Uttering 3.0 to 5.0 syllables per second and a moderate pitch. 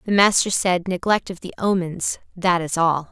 Yes: 4.7 syllables/s; medium, 180 Hz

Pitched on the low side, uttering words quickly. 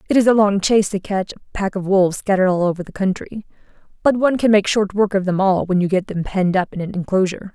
No: high, 195 Hz; fast, 270 wpm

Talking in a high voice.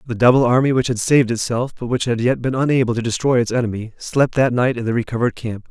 No: low, 120 Hz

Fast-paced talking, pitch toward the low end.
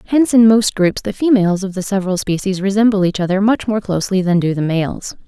No: fast, 230 wpm; high, 200 Hz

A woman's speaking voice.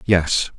No: male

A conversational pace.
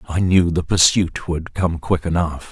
Yes: average, 190 wpm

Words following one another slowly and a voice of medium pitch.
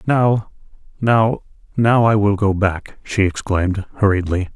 No: slow, 105 wpm; low, 105 Hz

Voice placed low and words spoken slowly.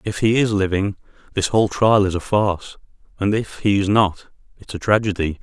No: low, 100 Hz; average, 200 wpm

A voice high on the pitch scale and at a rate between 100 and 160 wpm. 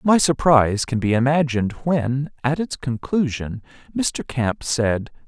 No: low, 135 Hz; slow, 135 wpm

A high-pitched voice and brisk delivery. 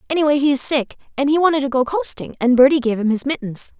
Yes: very high, 270 Hz; fast, 255 wpm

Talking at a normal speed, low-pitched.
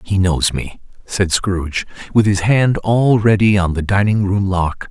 Yes: average, 170 wpm; low, 100 Hz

